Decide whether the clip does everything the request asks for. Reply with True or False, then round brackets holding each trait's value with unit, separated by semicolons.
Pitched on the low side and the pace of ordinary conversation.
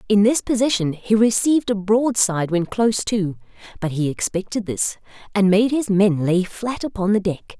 False (205 Hz; 180 wpm)